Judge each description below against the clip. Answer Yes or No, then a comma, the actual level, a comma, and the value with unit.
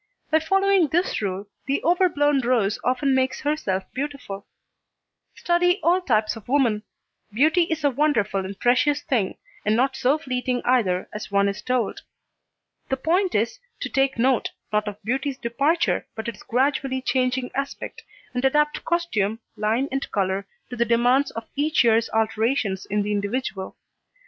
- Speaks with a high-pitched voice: Yes, very high, 255 Hz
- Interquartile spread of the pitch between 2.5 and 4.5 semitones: No, average, 5.3 semitones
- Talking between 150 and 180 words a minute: Yes, average, 155 wpm